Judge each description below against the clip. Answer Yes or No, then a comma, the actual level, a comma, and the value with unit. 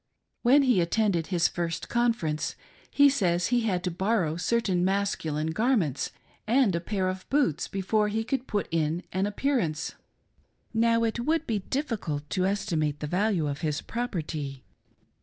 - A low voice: No, high, 190 Hz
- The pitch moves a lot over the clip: Yes, wide, 5.8 semitones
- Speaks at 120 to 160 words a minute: Yes, average, 155 wpm